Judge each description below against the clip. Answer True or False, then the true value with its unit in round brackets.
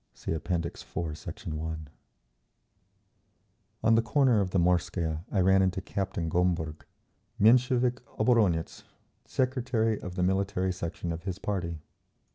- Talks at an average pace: False (125 wpm)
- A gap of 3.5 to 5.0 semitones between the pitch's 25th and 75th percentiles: True (4.6 semitones)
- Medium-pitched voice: False (95 Hz)